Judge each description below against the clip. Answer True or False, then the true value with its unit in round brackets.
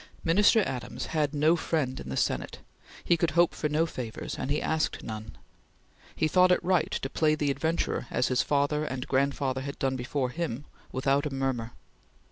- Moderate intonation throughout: True (3.4 semitones)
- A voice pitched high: False (145 Hz)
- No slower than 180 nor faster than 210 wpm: True (185 wpm)